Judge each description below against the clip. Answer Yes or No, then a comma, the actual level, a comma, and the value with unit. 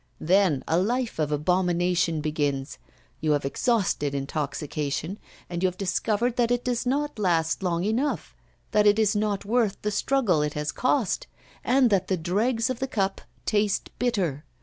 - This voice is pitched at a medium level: No, high, 195 Hz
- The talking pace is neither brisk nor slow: Yes, average, 165 wpm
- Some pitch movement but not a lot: No, wide, 6.3 semitones